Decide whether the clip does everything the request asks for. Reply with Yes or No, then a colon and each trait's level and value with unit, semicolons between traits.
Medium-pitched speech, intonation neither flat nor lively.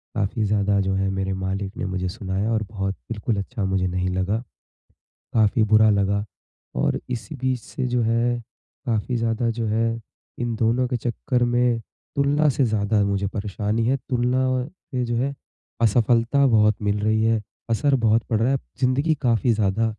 No: low, 115 Hz; average, 3.2 semitones